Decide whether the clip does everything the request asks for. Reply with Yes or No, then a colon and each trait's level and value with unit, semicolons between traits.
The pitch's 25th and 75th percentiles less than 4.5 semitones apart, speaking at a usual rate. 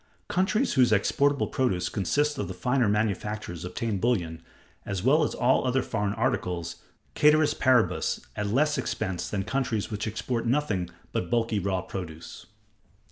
No: wide, 5.6 semitones; average, 145 wpm